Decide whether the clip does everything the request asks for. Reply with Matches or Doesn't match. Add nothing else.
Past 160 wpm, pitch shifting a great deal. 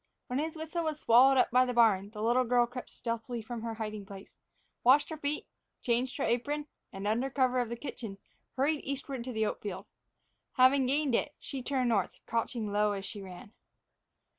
Doesn't match